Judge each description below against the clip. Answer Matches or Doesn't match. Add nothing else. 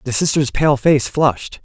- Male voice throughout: Matches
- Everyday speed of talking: Matches